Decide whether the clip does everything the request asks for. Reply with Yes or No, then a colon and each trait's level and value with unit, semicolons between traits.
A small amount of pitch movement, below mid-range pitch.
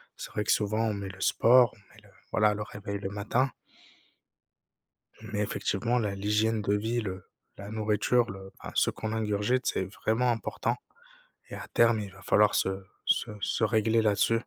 Yes: narrow, 1.9 semitones; low, 105 Hz